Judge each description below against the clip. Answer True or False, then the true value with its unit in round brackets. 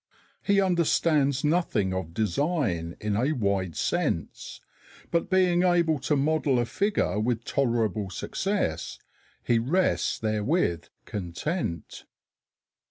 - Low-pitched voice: True (125 Hz)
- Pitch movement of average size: False (8.8 semitones)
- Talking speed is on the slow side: True (105 wpm)